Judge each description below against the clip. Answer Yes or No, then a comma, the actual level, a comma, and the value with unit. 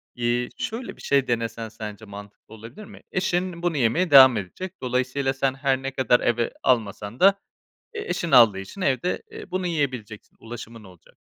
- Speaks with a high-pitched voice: No, low, 130 Hz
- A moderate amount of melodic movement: No, wide, 6.9 semitones